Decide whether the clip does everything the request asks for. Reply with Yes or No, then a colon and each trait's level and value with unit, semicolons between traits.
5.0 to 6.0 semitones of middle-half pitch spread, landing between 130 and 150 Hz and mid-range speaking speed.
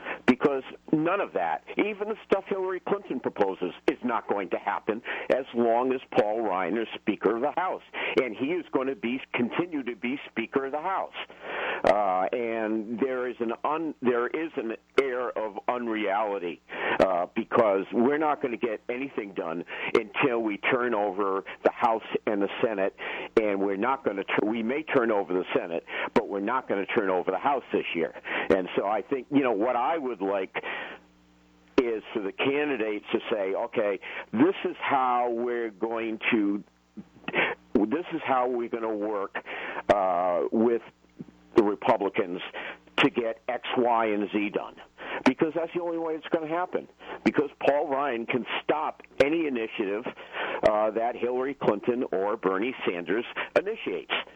No: average, 5.3 semitones; low, 120 Hz; average, 170 wpm